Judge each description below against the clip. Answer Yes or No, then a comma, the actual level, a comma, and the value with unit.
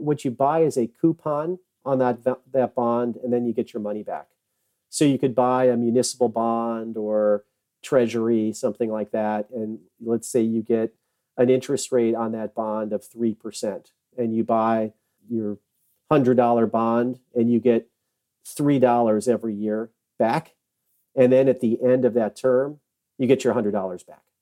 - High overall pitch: No, low, 120 Hz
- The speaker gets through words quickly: No, average, 165 wpm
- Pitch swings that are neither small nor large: No, narrow, 2.2 semitones